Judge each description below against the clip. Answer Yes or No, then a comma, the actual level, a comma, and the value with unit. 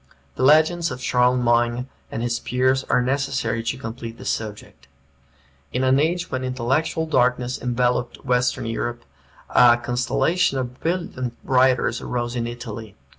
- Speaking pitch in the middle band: No, low, 125 Hz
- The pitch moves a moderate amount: No, narrow, 1.7 semitones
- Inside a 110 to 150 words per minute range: Yes, slow, 135 wpm